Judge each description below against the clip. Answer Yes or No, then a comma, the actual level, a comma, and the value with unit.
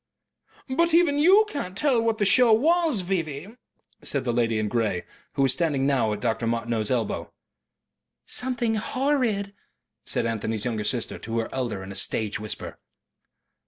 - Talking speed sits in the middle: Yes, average, 160 wpm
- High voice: No, medium, 140 Hz